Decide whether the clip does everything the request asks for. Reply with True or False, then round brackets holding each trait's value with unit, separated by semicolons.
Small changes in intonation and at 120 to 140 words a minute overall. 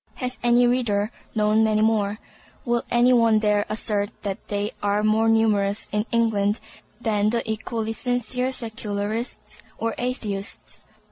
True (2.2 semitones; 135 wpm)